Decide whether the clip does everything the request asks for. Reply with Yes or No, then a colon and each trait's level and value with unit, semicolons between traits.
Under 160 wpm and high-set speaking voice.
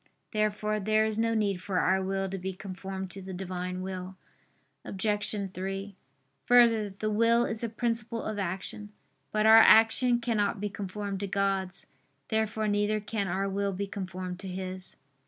No: average, 165 wpm; high, 200 Hz